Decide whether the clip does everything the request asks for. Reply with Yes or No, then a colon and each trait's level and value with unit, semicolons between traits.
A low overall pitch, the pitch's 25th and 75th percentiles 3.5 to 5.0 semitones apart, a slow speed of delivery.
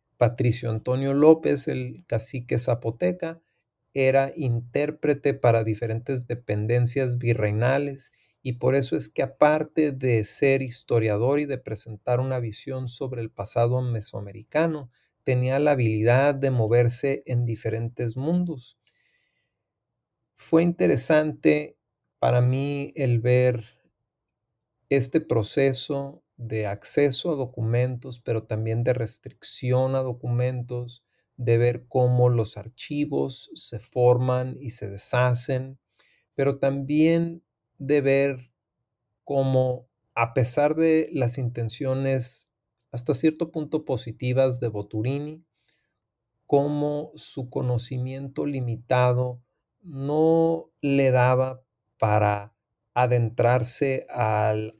No: low, 125 Hz; average, 2.9 semitones; slow, 100 wpm